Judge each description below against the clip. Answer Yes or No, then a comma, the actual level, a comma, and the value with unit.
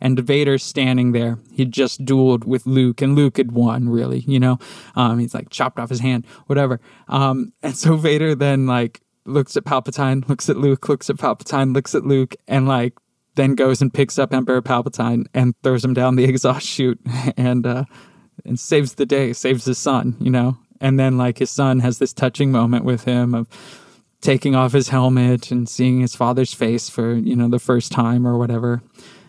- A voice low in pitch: Yes, low, 130 Hz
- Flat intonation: Yes, narrow, 1.7 semitones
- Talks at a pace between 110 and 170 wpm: No, average, 200 wpm